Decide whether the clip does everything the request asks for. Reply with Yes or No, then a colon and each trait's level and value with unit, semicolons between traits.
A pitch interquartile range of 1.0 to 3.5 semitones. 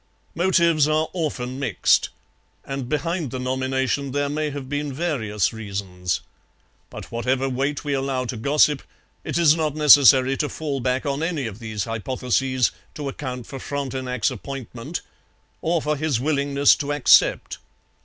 Yes: average, 2.8 semitones